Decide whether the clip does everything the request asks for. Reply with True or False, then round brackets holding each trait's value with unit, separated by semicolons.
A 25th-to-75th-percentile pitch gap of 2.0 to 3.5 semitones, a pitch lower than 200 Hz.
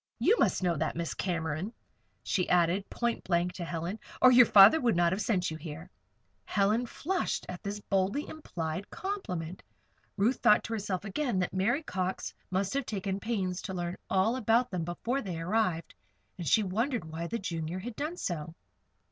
False (4.8 semitones; 190 Hz)